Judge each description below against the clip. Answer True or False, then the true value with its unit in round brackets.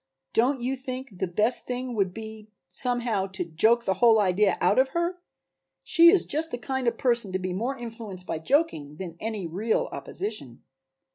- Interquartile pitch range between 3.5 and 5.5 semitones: True (5.1 semitones)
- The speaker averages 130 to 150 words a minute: False (190 wpm)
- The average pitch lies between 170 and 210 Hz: False (225 Hz)